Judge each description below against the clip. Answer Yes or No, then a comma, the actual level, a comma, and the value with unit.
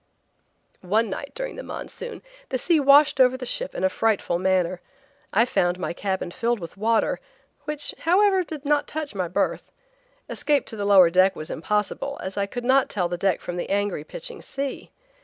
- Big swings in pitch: Yes, wide, 7.1 semitones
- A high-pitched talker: Yes, high, 220 Hz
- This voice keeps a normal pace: Yes, average, 190 wpm